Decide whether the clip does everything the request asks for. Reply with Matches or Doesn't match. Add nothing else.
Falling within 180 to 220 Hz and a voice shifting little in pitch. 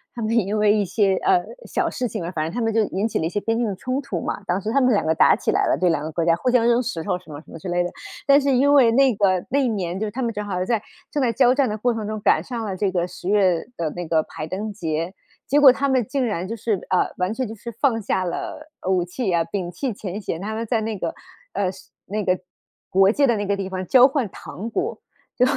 Doesn't match